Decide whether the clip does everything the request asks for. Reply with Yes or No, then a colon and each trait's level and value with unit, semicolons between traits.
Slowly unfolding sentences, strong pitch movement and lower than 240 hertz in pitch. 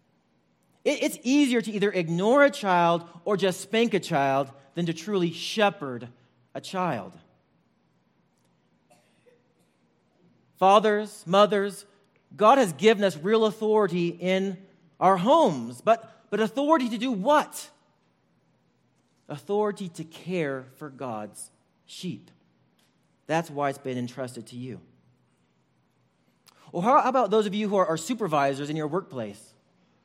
Yes: slow, 125 wpm; wide, 7.3 semitones; medium, 185 Hz